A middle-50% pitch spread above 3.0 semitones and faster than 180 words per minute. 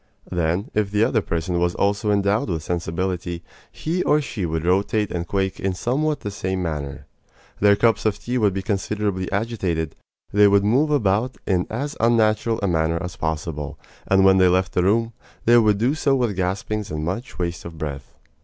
Yes: average, 3.9 semitones; average, 190 wpm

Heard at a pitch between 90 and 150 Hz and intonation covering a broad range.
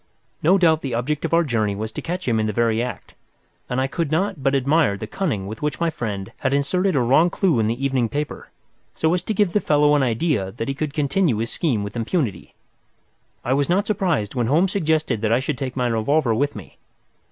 Yes: medium, 140 Hz; wide, 6.0 semitones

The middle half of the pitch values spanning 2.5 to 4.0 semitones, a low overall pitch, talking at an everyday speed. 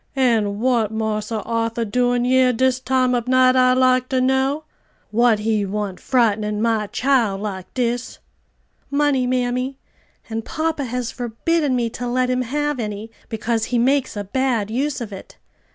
No: average, 2.8 semitones; high, 245 Hz; average, 160 wpm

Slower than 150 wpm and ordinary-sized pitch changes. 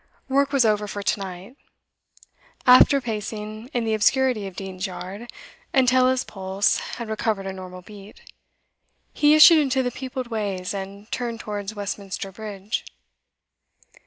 Yes: average, 140 wpm; average, 4.3 semitones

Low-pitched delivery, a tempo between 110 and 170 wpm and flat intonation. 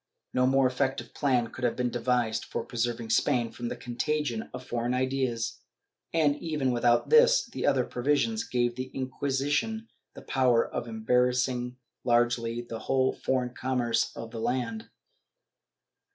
Yes: low, 125 Hz; average, 150 wpm; narrow, 2.0 semitones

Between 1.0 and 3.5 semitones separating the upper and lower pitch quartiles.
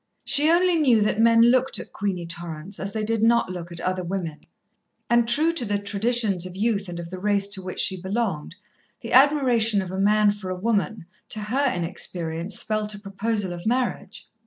No: average, 4.0 semitones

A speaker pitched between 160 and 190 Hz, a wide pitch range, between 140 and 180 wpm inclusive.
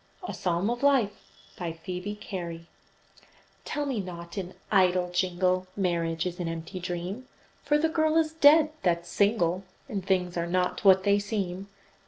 No: medium, 185 Hz; average, 3.3 semitones; average, 160 wpm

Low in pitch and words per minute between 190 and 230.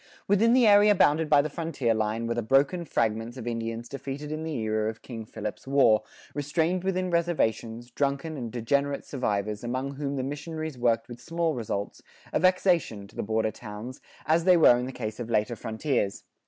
Yes: low, 130 Hz; average, 195 wpm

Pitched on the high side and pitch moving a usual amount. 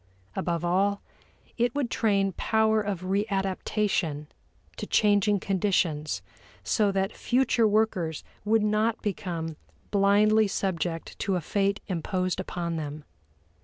Yes: high, 195 Hz; average, 3.2 semitones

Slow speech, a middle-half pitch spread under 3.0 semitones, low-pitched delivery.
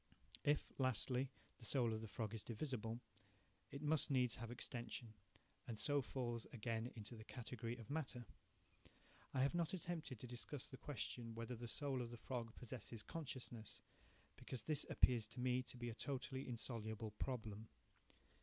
No: average, 165 wpm; narrow, 2.6 semitones; low, 120 Hz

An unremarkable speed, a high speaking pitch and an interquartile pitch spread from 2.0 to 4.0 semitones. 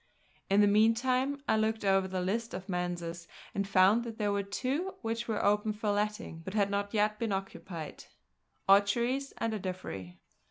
Yes: average, 170 wpm; high, 205 Hz; average, 2.8 semitones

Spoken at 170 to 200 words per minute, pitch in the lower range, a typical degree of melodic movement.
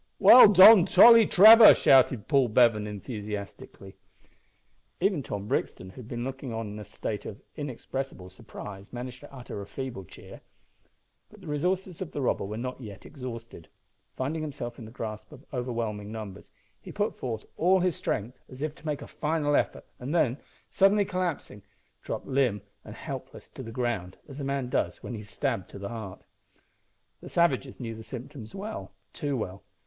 No: average, 180 wpm; low, 125 Hz; wide, 5.7 semitones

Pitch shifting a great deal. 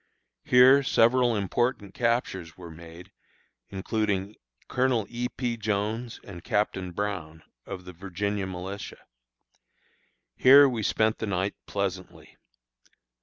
No: average, 4.0 semitones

